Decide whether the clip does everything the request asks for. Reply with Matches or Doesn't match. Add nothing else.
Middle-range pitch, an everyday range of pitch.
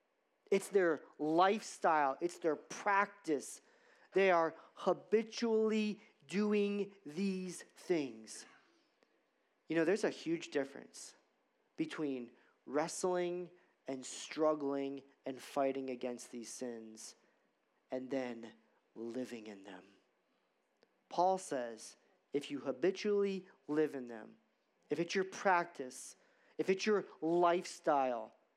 Doesn't match